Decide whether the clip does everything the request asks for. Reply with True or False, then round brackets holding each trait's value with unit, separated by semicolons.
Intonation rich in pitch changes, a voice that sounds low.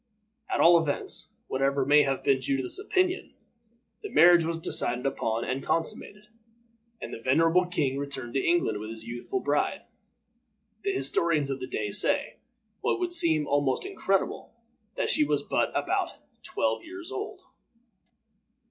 False (6.2 semitones; 145 Hz)